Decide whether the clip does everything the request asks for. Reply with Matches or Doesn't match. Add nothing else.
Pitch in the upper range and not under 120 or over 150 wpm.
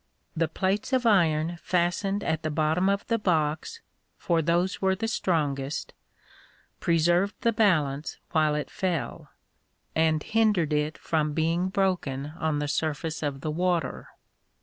Doesn't match